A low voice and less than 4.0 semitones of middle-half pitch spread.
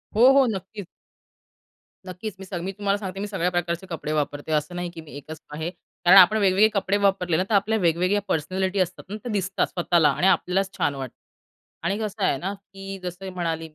No: medium, 185 Hz; average, 2.7 semitones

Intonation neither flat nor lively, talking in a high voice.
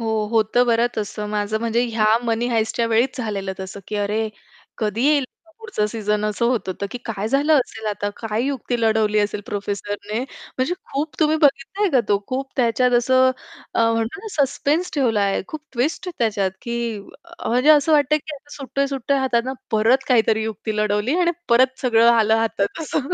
Yes: average, 4.0 semitones; high, 235 Hz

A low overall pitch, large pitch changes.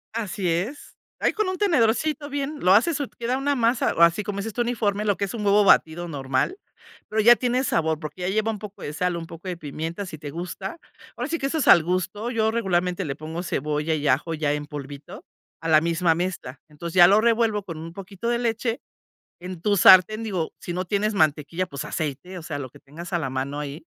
No: medium, 185 Hz; wide, 5.7 semitones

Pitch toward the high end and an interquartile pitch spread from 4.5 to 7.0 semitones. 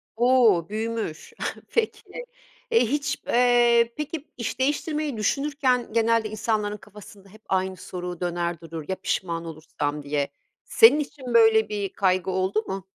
Yes: high, 215 Hz; average, 4.8 semitones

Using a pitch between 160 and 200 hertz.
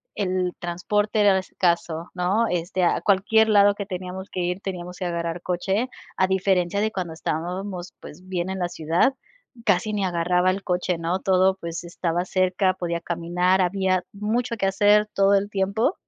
Yes: medium, 185 Hz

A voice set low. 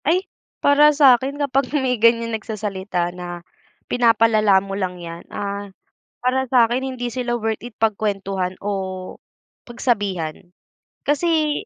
No: high, 225 Hz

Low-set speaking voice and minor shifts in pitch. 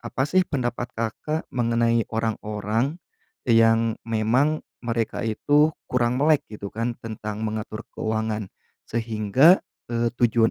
Yes: low, 115 Hz; narrow, 2.0 semitones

